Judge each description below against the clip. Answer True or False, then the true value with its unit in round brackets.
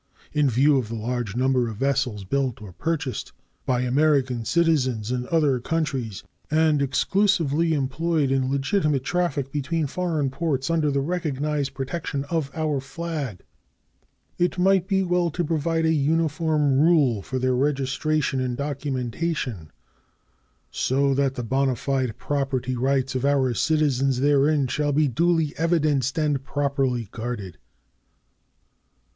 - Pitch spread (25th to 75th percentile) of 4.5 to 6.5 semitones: False (3.4 semitones)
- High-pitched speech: False (140 Hz)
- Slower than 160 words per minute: True (135 wpm)